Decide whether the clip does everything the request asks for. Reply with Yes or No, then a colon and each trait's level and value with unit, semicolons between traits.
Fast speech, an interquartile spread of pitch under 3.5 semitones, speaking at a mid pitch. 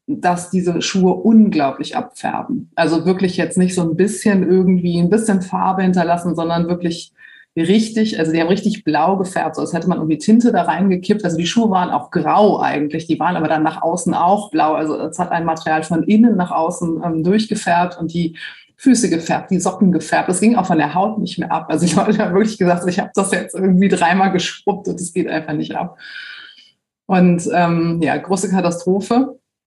Yes: fast, 200 wpm; average, 2.9 semitones; medium, 180 Hz